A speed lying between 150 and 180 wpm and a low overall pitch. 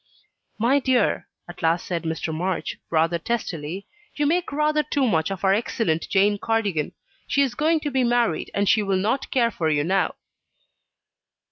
No: average, 170 wpm; high, 205 Hz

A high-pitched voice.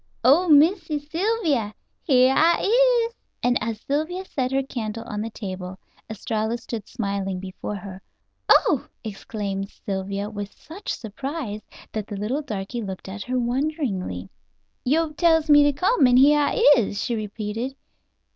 Yes: high, 240 Hz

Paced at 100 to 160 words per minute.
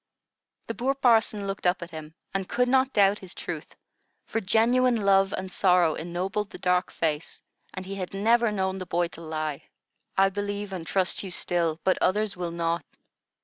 No: average, 185 wpm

